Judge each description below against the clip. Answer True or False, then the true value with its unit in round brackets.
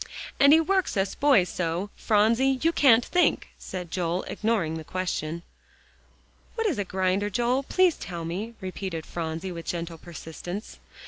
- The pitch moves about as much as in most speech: False (6.2 semitones)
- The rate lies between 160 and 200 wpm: False (150 wpm)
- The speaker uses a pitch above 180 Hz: True (190 Hz)